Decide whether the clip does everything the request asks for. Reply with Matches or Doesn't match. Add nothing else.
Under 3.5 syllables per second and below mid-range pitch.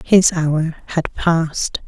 Doesn't match